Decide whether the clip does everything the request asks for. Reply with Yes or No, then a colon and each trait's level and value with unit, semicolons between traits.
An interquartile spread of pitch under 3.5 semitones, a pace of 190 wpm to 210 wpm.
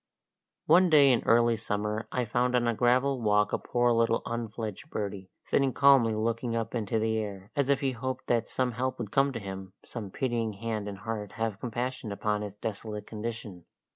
Yes: average, 3.0 semitones; average, 195 wpm